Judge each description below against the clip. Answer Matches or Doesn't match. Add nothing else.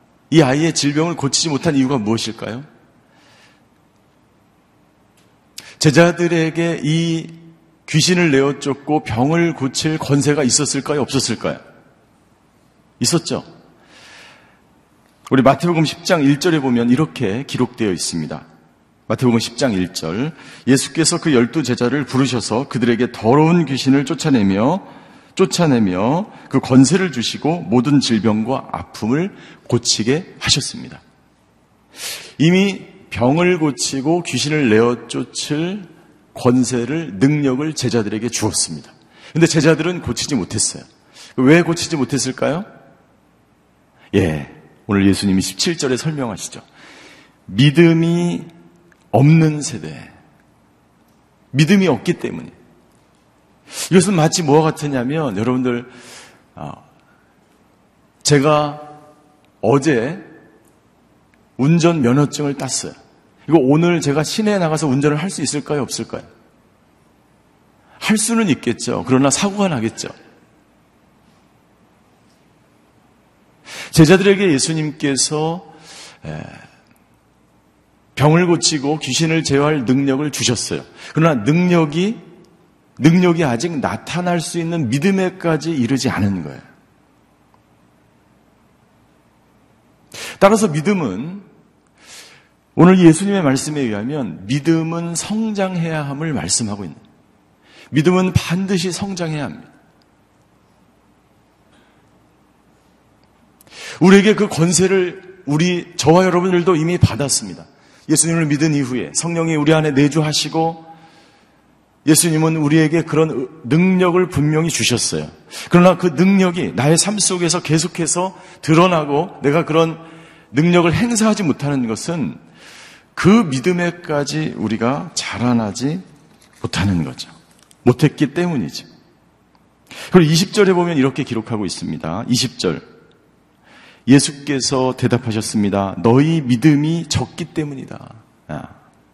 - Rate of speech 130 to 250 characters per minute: Matches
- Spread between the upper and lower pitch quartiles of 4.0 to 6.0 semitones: Matches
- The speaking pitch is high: Doesn't match